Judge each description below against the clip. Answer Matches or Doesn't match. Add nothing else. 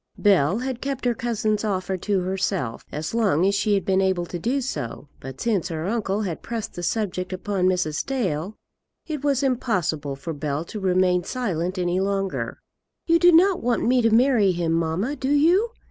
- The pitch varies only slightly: Doesn't match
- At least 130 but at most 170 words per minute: Doesn't match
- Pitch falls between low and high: Doesn't match